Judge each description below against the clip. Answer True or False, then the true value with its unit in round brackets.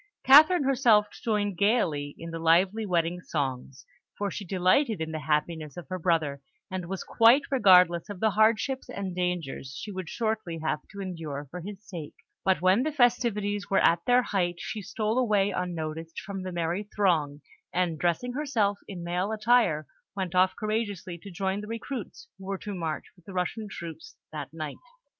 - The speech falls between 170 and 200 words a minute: True (180 wpm)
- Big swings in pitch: False (4.1 semitones)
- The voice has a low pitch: False (190 Hz)